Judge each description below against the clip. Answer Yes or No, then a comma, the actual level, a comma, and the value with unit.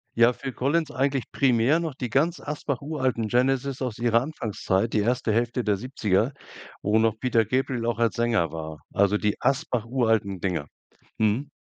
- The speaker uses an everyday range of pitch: Yes, average, 3.7 semitones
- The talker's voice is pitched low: Yes, low, 120 Hz